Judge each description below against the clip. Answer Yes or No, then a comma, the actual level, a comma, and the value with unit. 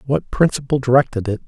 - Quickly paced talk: No, average, 165 wpm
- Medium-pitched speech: No, low, 130 Hz